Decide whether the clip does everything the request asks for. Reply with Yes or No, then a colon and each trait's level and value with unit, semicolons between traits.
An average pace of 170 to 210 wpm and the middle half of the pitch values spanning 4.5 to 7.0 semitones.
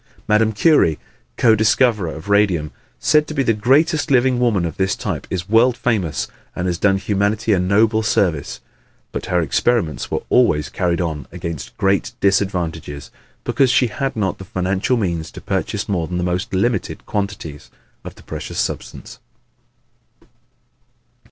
No: average, 155 wpm; average, 4.8 semitones